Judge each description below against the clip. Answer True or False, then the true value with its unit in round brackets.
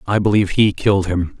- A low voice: True (100 Hz)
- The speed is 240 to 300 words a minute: False (215 wpm)